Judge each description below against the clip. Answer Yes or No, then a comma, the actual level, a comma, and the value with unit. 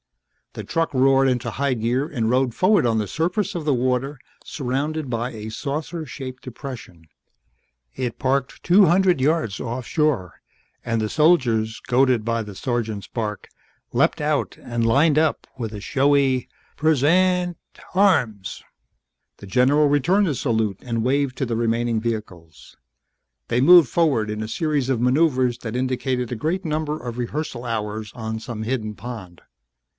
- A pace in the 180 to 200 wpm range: No, average, 155 wpm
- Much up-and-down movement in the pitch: No, average, 4.6 semitones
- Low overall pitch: Yes, low, 125 Hz